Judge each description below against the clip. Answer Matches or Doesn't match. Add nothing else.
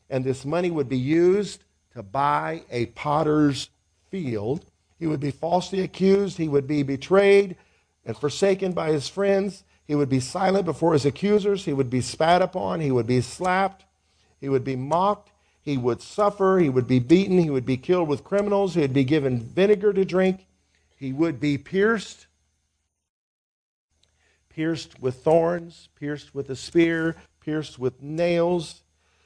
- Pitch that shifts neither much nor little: Doesn't match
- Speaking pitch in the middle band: Matches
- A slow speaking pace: Doesn't match